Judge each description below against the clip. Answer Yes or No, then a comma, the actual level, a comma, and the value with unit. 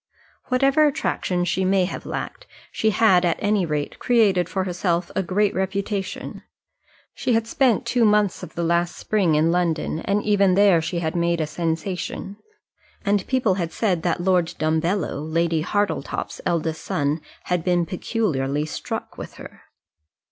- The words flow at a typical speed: Yes, average, 155 wpm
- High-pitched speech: No, medium, 180 Hz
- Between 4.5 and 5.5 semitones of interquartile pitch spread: No, average, 3.5 semitones